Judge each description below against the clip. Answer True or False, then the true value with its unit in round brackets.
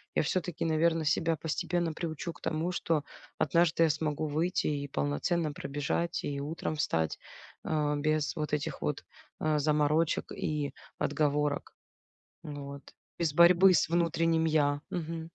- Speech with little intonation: True (2.1 semitones)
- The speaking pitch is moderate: True (155 Hz)